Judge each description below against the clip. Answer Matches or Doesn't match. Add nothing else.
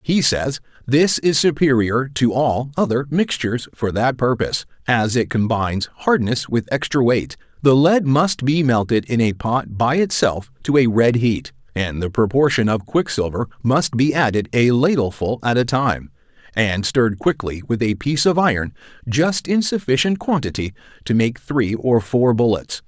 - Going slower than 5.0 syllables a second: Matches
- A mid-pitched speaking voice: Doesn't match